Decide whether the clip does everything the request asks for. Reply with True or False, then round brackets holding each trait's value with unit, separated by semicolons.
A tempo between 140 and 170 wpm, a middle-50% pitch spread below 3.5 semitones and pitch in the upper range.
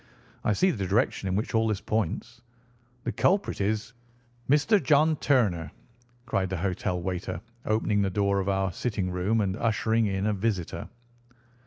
False (160 wpm; 3.1 semitones; 105 Hz)